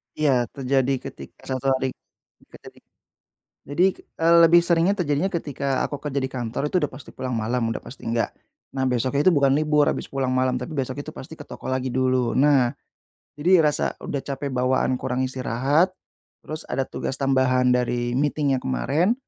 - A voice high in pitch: No, low, 135 Hz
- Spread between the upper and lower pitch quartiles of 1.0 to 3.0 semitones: Yes, narrow, 2.6 semitones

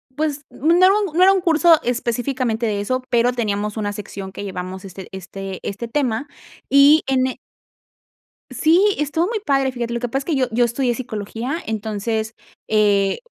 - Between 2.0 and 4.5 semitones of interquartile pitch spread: No, average, 5.2 semitones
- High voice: Yes, high, 240 Hz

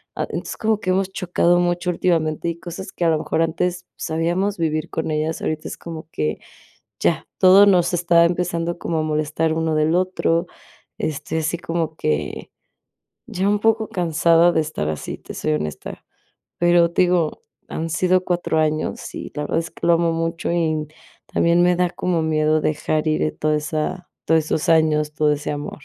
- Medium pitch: Yes, medium, 165 Hz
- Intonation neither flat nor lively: No, narrow, 2.1 semitones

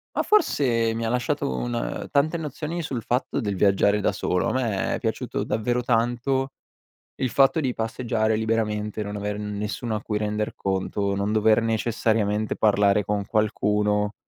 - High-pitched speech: No, low, 110 Hz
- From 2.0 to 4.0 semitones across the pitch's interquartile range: Yes, average, 2.7 semitones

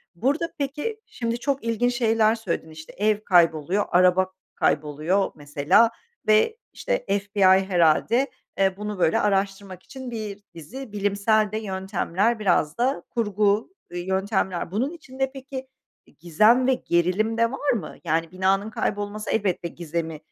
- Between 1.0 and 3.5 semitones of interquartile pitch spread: No, average, 4.2 semitones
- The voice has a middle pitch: No, high, 205 Hz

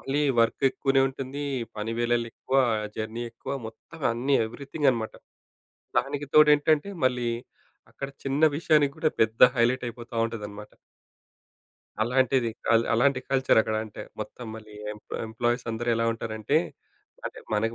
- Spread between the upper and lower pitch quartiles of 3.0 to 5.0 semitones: Yes, average, 3.3 semitones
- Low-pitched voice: Yes, low, 120 Hz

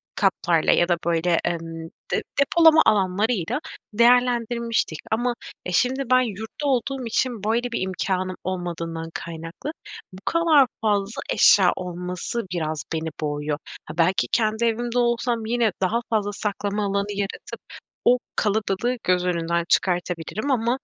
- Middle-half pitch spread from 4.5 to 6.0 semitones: Yes, average, 5.2 semitones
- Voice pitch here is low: No, high, 205 Hz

